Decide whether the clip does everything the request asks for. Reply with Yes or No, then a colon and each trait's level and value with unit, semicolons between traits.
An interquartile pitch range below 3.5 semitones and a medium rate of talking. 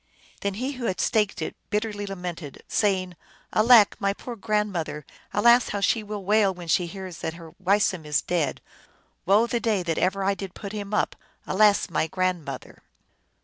Yes: average, 3.0 semitones; average, 185 wpm